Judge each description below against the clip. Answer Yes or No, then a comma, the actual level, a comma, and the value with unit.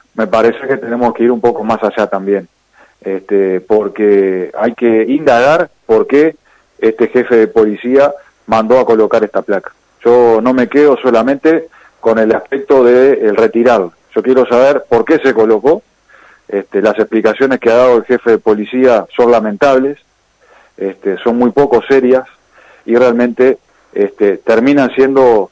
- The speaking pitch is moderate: No, low, 120 Hz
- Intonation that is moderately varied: Yes, average, 3.1 semitones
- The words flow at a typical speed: Yes, average, 160 wpm